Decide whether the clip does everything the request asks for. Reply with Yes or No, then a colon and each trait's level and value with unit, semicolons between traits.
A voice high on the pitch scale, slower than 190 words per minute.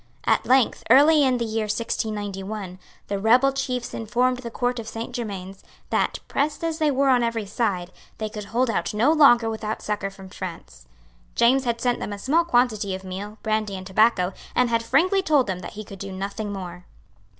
No: high, 225 Hz; average, 195 wpm